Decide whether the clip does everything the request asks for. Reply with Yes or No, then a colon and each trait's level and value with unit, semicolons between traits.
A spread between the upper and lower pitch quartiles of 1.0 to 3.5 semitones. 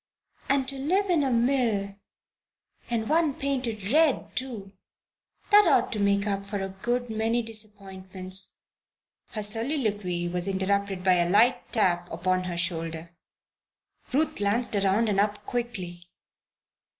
No: average, 4.4 semitones